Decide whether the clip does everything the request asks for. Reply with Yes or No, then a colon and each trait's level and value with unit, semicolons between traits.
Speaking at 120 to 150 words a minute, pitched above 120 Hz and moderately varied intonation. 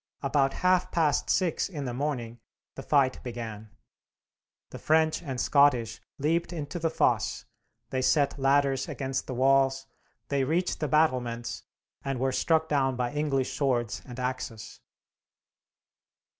Yes: slow, 135 wpm; low, 135 Hz; average, 3.0 semitones